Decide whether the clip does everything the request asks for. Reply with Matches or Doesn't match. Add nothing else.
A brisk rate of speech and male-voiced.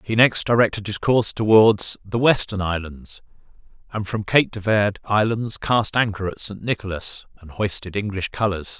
Doesn't match